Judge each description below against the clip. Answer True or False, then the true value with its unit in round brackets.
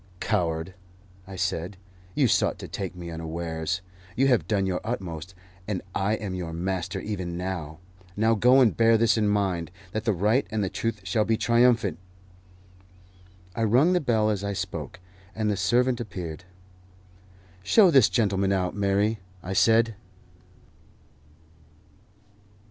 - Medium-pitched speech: False (100 Hz)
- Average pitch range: True (3.8 semitones)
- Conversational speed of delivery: True (145 wpm)